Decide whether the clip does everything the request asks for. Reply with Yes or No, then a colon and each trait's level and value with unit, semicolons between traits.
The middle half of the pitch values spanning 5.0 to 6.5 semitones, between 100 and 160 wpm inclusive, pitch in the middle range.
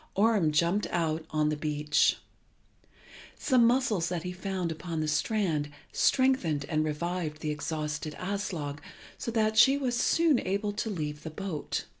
Yes: wide, 5.5 semitones; average, 150 wpm; medium, 170 Hz